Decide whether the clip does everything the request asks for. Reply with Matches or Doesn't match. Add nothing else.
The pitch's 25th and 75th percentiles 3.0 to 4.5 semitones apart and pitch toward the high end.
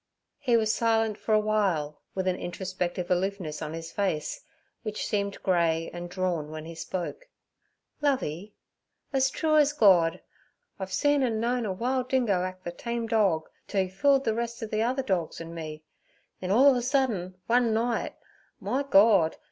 Doesn't match